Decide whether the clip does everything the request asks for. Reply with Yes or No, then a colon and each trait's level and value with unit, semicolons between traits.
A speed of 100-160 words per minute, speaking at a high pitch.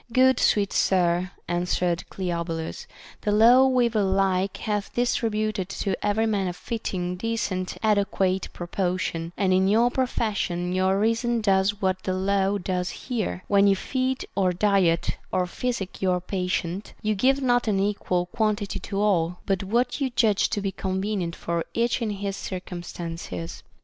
Yes: average, 155 wpm; high, 195 Hz